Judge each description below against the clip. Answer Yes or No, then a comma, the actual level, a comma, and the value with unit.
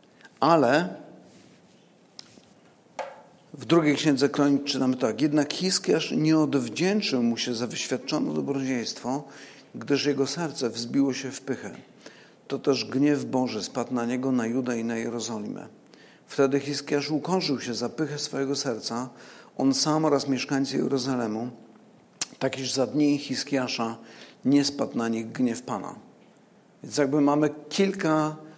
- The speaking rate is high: No, average, 130 wpm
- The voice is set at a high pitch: No, medium, 140 Hz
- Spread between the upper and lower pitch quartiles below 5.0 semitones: Yes, average, 3.1 semitones